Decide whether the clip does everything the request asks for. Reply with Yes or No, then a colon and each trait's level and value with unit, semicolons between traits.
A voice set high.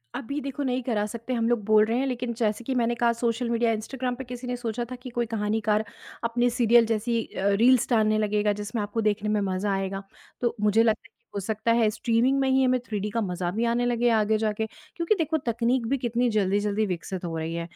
Yes: high, 230 Hz